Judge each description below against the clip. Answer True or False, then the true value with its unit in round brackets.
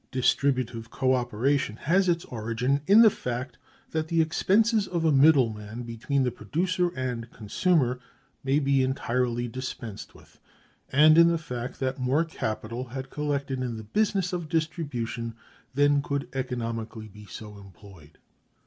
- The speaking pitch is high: False (130 Hz)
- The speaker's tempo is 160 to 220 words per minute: False (150 wpm)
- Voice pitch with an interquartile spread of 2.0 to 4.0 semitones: False (5.1 semitones)